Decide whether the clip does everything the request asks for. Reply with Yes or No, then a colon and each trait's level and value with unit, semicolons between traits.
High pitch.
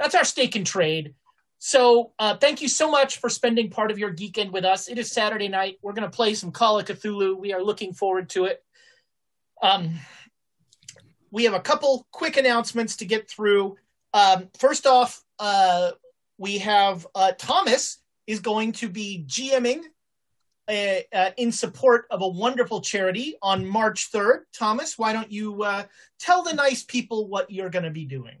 Yes: high, 215 Hz